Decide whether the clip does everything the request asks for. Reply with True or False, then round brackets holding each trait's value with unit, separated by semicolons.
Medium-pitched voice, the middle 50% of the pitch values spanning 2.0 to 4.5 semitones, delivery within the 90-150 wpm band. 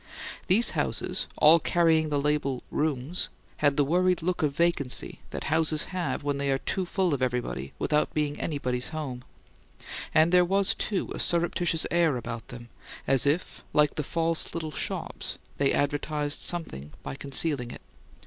False (150 Hz; 3.5 semitones; 160 wpm)